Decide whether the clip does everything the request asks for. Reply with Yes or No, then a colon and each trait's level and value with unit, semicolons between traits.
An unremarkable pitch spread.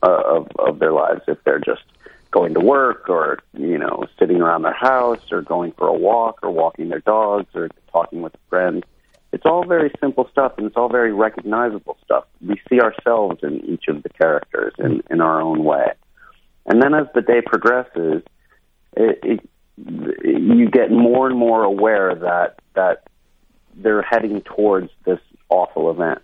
No: wide, 5.8 semitones